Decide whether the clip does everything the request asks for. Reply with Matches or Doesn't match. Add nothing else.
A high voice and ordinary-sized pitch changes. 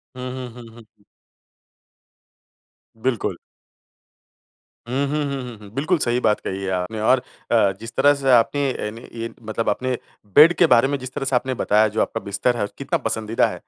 Doesn't match